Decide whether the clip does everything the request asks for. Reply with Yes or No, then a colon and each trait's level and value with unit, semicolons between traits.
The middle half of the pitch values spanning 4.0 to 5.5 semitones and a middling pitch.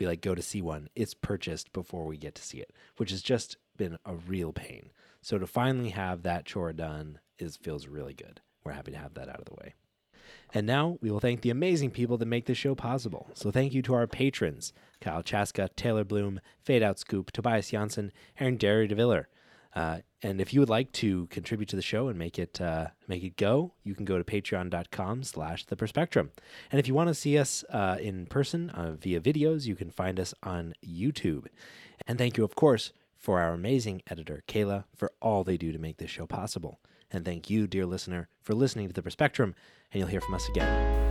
No: average, 5.2 semitones; low, 100 Hz